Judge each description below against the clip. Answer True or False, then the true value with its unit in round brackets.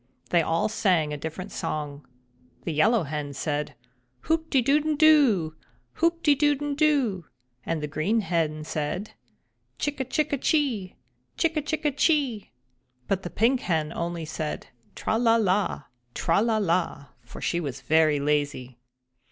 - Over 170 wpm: False (150 wpm)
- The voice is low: False (190 Hz)